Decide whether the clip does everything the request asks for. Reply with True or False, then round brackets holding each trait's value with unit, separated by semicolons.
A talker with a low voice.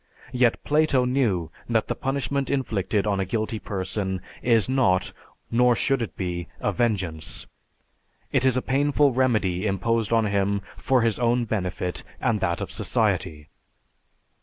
True (115 Hz)